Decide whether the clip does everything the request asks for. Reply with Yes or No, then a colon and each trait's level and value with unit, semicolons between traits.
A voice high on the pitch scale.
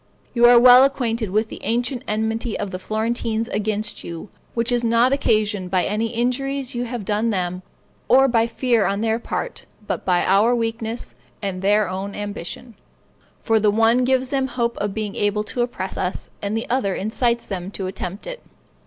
Yes: high, 225 Hz